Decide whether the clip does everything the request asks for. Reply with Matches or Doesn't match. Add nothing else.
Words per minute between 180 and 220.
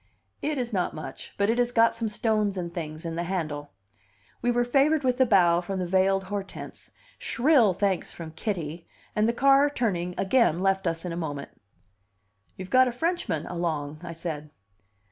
Matches